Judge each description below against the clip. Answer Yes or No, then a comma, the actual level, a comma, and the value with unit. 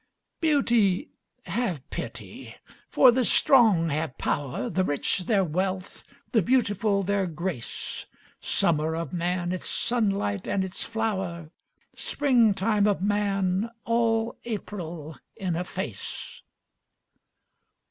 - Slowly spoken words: Yes, slow, 110 wpm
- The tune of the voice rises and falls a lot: No, average, 4.6 semitones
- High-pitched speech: Yes, high, 195 Hz